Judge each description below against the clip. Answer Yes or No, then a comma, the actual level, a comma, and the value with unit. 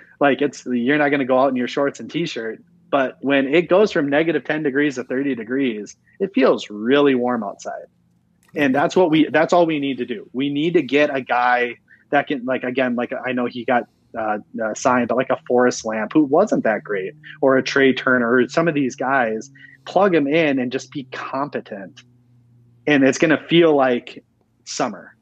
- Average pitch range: Yes, average, 3.2 semitones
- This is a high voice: No, low, 135 Hz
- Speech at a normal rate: No, fast, 210 wpm